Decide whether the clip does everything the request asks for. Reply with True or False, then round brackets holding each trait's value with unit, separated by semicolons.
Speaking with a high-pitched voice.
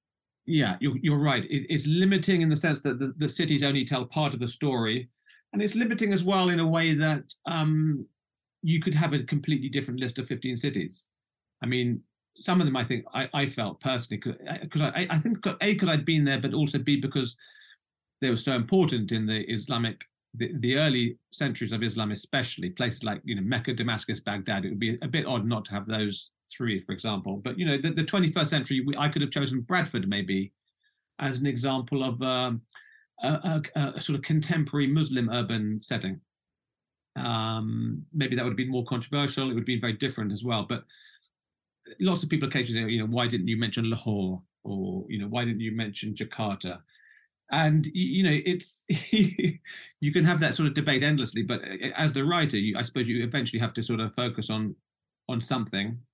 False (135 Hz)